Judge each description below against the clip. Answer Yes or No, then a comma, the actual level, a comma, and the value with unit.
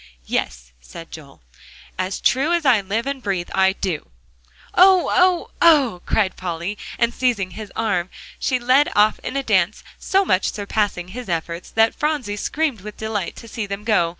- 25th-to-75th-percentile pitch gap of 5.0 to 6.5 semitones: Yes, wide, 5.6 semitones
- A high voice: Yes, high, 210 Hz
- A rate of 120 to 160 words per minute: No, average, 175 wpm